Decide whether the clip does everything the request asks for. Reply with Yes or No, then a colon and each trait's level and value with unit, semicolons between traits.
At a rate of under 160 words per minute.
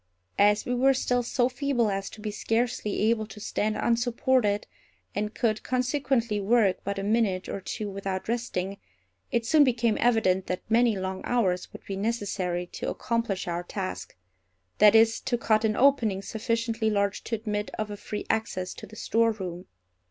No: average, 165 wpm